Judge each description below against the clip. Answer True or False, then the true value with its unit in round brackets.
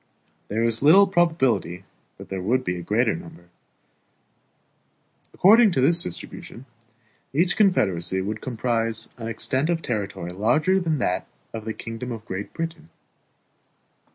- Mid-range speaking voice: False (115 Hz)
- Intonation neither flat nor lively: False (7.8 semitones)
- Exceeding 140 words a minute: False (135 wpm)